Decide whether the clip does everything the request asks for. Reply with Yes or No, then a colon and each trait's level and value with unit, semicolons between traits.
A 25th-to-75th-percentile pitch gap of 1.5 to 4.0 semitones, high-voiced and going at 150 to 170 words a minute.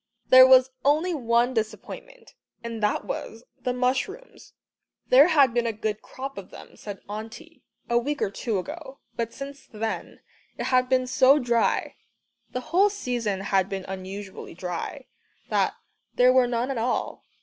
Yes: average, 3.7 semitones; very high, 250 Hz; average, 160 wpm